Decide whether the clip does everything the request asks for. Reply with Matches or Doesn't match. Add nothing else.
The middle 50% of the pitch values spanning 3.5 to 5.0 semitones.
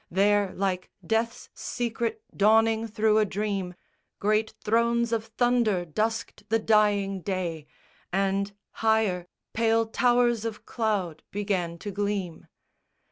Doesn't match